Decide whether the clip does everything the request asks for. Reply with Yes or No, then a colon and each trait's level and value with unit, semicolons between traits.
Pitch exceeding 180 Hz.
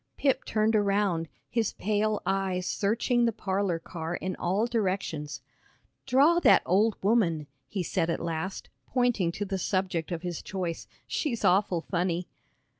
Yes: high, 190 Hz